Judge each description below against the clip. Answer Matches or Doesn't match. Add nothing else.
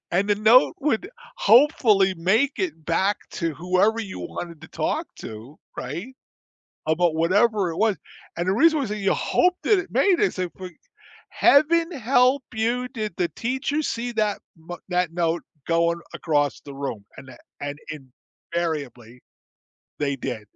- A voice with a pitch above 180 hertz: Matches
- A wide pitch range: Matches